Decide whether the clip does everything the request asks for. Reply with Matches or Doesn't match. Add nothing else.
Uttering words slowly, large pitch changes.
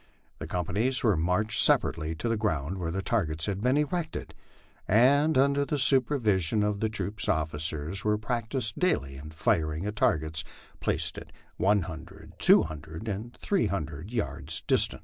Doesn't match